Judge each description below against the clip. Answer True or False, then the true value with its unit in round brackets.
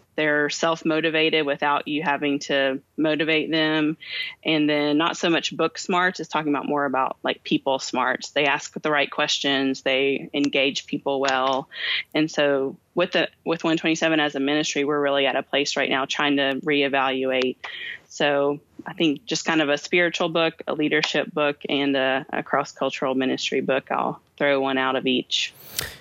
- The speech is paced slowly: False (175 wpm)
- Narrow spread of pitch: True (2.3 semitones)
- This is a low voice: False (145 Hz)